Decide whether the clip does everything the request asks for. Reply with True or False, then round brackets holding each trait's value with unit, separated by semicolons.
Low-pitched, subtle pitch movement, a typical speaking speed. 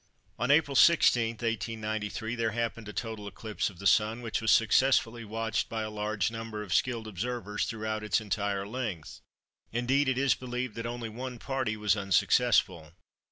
True (115 Hz; 2.3 semitones; 165 wpm)